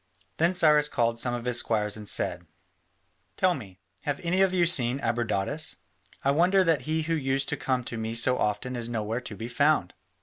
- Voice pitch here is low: Yes, low, 125 Hz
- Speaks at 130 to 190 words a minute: No, average, 200 wpm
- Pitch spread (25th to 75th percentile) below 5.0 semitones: No, average, 5.3 semitones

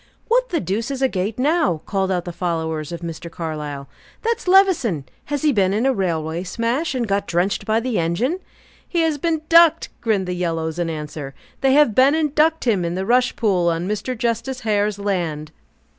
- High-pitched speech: Yes, high, 205 Hz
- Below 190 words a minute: No, average, 200 wpm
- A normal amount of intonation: No, wide, 7.9 semitones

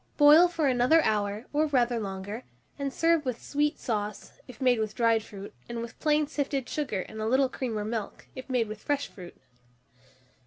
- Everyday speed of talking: Yes, average, 190 wpm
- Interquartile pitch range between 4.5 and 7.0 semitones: Yes, average, 5.0 semitones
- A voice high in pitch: Yes, high, 245 Hz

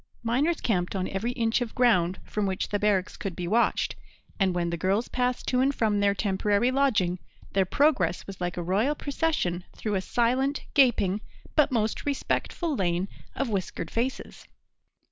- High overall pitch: Yes, high, 210 Hz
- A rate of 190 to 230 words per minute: No, average, 170 wpm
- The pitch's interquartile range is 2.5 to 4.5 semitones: No, average, 5.1 semitones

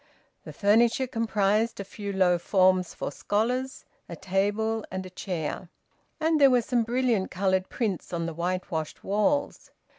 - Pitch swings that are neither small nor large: Yes, average, 3.9 semitones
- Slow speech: No, average, 150 wpm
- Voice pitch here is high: Yes, high, 200 Hz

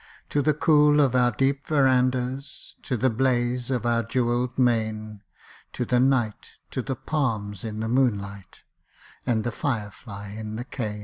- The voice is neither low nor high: No, low, 120 Hz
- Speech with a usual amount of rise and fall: Yes, average, 3.2 semitones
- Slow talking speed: No, average, 165 wpm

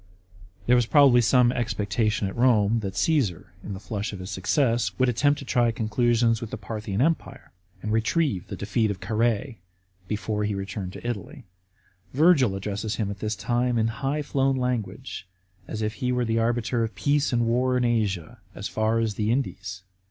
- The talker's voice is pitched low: Yes, low, 115 Hz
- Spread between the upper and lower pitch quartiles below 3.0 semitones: No, average, 3.3 semitones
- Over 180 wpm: Yes, average, 190 wpm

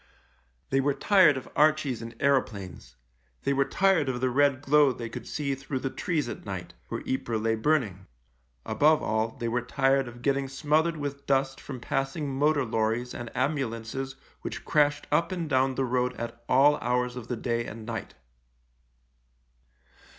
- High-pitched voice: No, low, 135 Hz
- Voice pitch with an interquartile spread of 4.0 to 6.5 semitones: No, average, 3.5 semitones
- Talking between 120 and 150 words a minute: No, average, 170 wpm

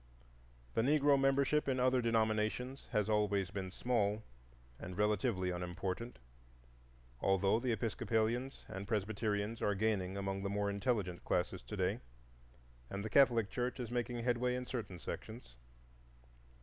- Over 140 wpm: No, slow, 135 wpm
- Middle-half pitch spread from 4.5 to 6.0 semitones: No, average, 3.7 semitones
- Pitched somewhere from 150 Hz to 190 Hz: No, low, 110 Hz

